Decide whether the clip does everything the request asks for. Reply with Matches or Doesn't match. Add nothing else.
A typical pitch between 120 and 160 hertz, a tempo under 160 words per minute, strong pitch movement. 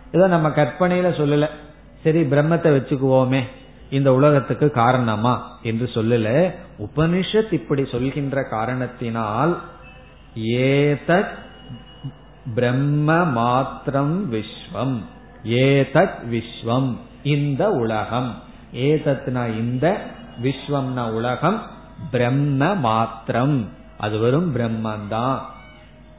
Doesn't match